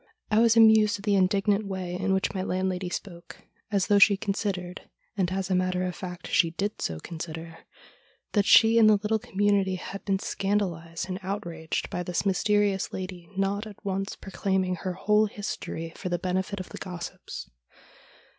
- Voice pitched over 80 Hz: Yes, high, 190 Hz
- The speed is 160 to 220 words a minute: Yes, average, 185 wpm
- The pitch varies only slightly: Yes, narrow, 2.1 semitones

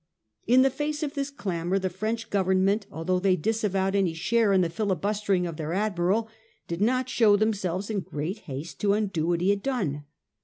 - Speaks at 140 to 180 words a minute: No, average, 195 wpm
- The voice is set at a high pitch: Yes, high, 195 Hz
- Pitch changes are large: No, average, 3.7 semitones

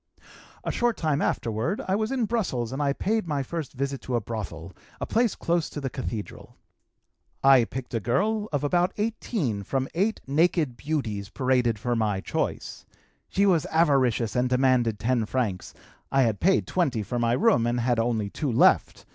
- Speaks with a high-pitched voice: No, low, 130 Hz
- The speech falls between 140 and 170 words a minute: No, average, 180 wpm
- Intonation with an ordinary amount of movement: No, wide, 6.5 semitones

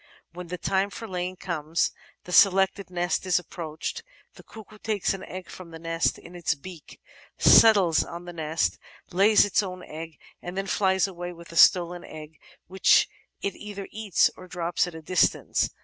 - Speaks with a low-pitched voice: No, medium, 180 Hz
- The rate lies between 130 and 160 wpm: No, average, 180 wpm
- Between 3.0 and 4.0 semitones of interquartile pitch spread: No, narrow, 2.4 semitones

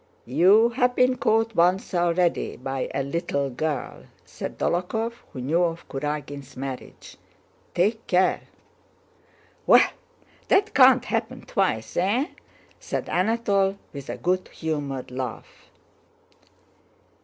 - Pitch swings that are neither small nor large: No, wide, 7.0 semitones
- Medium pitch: Yes, medium, 175 Hz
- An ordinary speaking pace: No, slow, 110 wpm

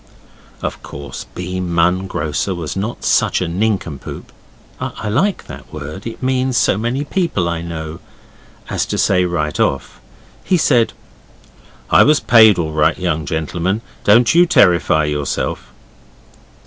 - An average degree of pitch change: No, wide, 6.3 semitones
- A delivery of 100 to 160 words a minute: Yes, average, 140 wpm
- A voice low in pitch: Yes, very low, 90 Hz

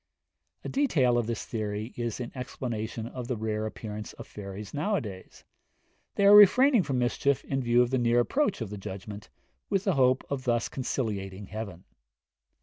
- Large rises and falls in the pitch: No, average, 4.1 semitones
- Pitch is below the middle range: Yes, low, 120 Hz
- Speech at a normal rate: Yes, average, 170 wpm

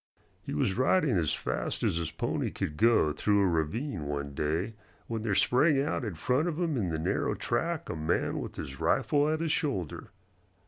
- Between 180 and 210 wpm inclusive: Yes, average, 195 wpm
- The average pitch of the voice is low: Yes, low, 105 Hz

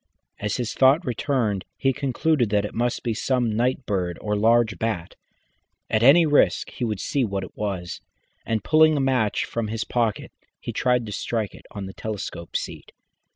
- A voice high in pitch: No, low, 115 Hz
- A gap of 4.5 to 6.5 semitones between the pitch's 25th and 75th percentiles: No, average, 3.7 semitones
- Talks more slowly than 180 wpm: No, average, 185 wpm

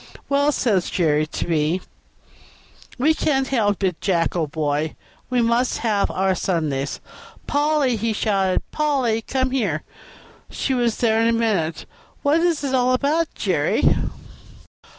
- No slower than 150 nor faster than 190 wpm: No, average, 140 wpm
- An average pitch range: No, wide, 7.0 semitones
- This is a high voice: Yes, high, 225 Hz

